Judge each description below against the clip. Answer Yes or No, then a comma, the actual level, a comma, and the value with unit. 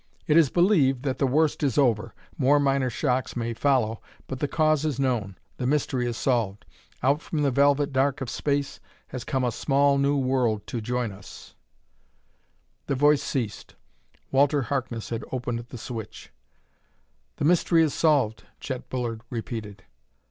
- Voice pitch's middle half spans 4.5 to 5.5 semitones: No, average, 3.1 semitones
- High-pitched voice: No, low, 130 Hz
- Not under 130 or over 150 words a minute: No, average, 165 wpm